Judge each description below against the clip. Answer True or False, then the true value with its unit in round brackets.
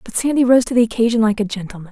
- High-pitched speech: True (225 Hz)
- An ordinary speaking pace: False (280 wpm)